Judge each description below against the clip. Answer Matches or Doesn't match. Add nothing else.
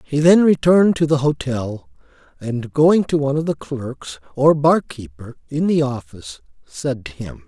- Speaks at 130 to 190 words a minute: Matches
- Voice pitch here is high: Doesn't match